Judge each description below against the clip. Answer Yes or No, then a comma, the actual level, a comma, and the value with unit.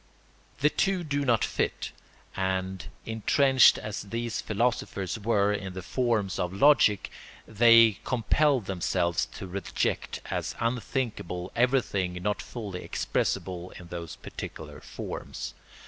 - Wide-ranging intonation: No, average, 4.4 semitones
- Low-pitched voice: Yes, low, 105 Hz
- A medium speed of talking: No, slow, 115 wpm